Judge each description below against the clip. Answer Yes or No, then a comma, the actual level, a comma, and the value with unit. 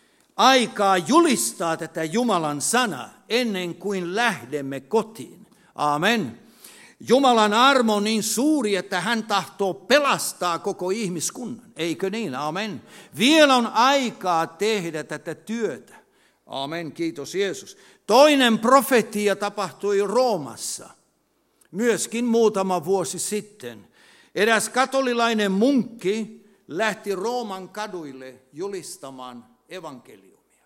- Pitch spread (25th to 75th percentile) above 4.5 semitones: Yes, average, 5.1 semitones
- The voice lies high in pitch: Yes, high, 205 Hz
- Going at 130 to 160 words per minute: No, slow, 95 wpm